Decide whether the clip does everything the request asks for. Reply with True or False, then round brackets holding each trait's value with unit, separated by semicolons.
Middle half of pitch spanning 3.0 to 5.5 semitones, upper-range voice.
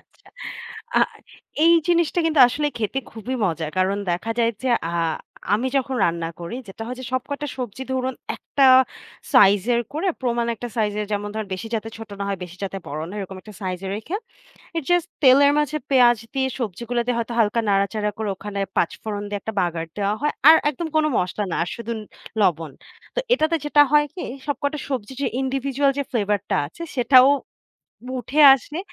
True (5.1 semitones; 235 Hz)